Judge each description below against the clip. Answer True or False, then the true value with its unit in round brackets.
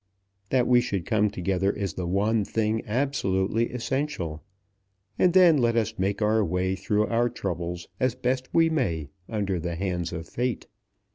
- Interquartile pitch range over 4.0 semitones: True (5.0 semitones)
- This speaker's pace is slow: False (160 wpm)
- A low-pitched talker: True (105 Hz)